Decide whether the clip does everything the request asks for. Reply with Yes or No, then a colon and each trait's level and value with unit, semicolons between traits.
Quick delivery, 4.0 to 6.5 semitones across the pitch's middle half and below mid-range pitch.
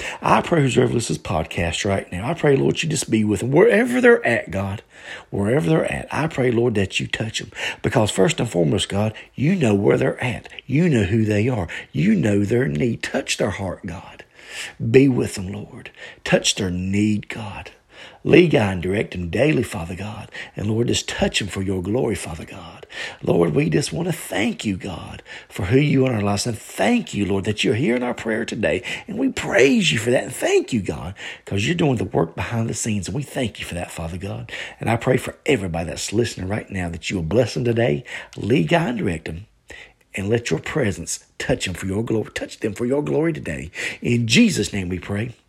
Yes: fast, 225 wpm; average, 4.6 semitones; low, 110 Hz